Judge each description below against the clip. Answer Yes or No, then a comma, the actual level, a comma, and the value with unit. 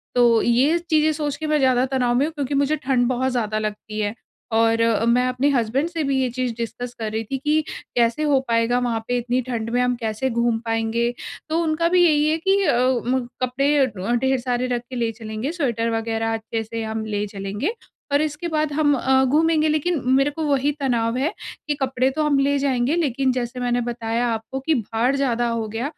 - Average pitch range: Yes, average, 3.7 semitones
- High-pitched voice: Yes, very high, 250 Hz